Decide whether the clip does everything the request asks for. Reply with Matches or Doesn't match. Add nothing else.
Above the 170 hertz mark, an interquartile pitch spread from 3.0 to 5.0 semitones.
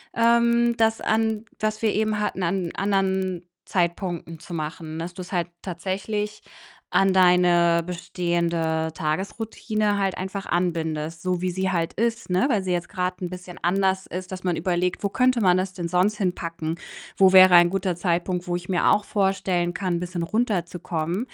Doesn't match